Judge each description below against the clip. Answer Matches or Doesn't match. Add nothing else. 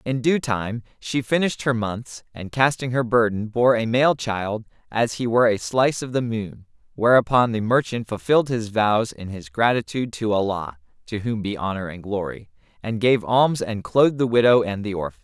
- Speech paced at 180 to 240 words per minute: Matches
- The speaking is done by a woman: Doesn't match